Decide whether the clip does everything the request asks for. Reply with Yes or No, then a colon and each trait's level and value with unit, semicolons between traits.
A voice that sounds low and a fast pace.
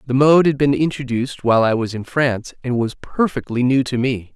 Yes: low, 130 Hz; fast, 220 wpm